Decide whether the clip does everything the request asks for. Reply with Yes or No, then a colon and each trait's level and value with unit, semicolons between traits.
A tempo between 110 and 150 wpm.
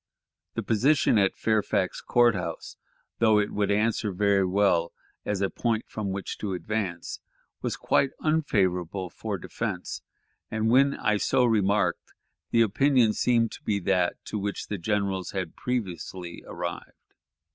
Yes: average, 145 wpm